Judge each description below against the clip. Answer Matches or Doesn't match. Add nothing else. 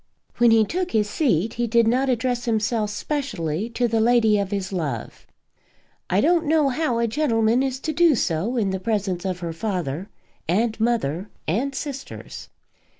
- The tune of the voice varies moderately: Matches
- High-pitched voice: Matches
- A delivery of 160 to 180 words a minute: Matches